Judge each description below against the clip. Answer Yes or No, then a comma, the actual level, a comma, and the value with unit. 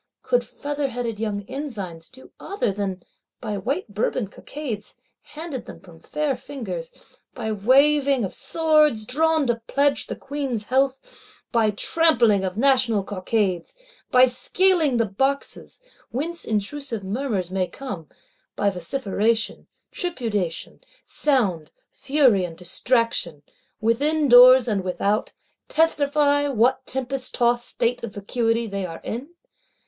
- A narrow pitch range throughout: No, wide, 5.5 semitones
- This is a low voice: No, high, 240 Hz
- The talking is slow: Yes, slow, 120 wpm